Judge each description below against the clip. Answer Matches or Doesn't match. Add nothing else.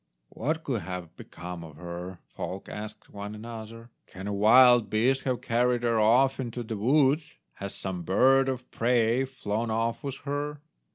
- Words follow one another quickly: Doesn't match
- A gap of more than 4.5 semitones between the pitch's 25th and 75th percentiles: Doesn't match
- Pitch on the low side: Matches